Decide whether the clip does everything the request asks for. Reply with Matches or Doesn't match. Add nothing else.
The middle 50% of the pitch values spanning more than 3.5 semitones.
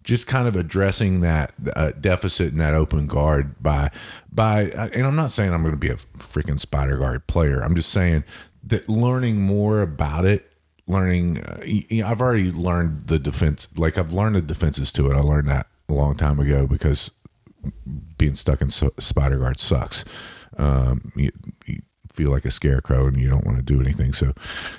Matches